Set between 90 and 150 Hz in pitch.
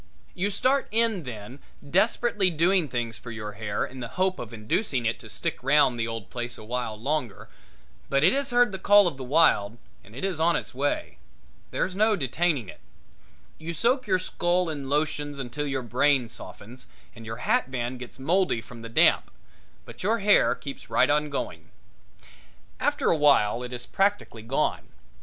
Yes: medium, 140 Hz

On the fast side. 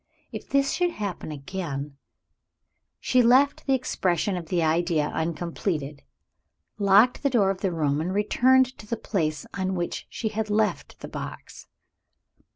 No: average, 155 wpm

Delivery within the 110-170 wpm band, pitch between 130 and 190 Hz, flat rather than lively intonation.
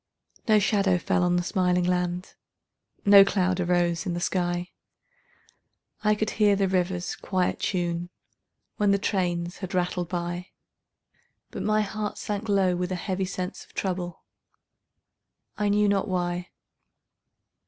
Yes: average, 140 wpm; medium, 185 Hz; narrow, 2.1 semitones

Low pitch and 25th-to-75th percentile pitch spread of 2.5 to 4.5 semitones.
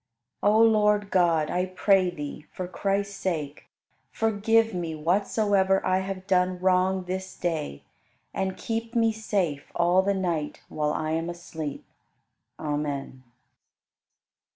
No: medium, 185 Hz; average, 3.7 semitones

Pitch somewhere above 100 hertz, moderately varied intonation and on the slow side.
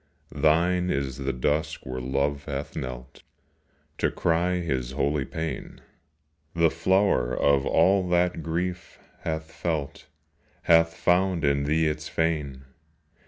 No: very low, 80 Hz; average, 3.7 semitones; slow, 120 wpm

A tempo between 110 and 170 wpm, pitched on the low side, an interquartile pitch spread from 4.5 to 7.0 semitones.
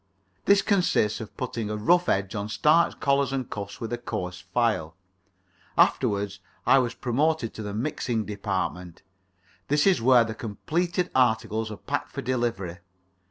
Yes: average, 155 wpm; low, 115 Hz; average, 5.0 semitones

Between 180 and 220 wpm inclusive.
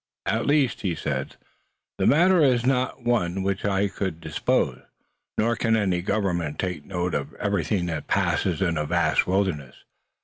No: average, 165 wpm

